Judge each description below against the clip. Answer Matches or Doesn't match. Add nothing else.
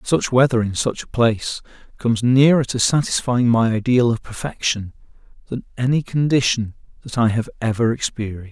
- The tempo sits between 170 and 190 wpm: Doesn't match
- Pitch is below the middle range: Matches